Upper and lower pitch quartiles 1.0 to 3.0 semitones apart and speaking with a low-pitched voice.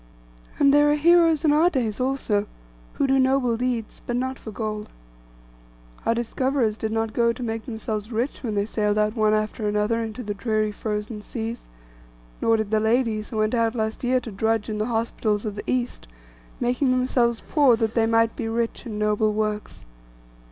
No: average, 2.7 semitones; high, 225 Hz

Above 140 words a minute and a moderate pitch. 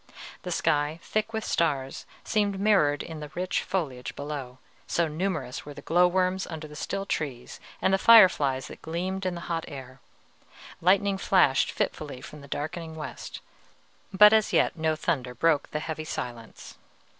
Yes: average, 165 wpm; medium, 160 Hz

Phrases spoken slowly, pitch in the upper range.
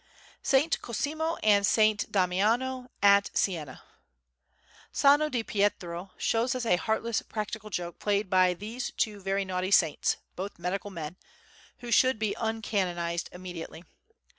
Yes: slow, 130 wpm; high, 205 Hz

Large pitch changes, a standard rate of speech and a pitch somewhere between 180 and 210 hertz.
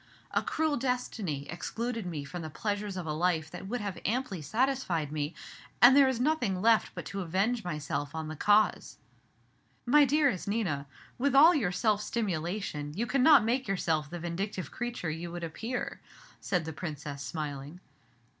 Yes: wide, 7.2 semitones; average, 165 wpm; high, 190 Hz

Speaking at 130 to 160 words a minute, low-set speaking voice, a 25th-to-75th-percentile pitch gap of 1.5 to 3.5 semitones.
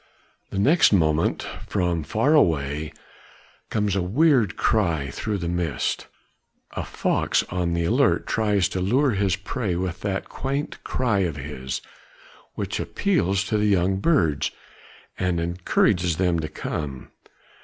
No: slow, 135 wpm; very low, 90 Hz; average, 4.0 semitones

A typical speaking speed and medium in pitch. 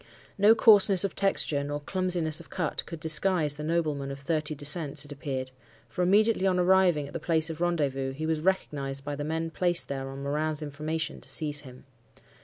Yes: average, 195 wpm; medium, 155 Hz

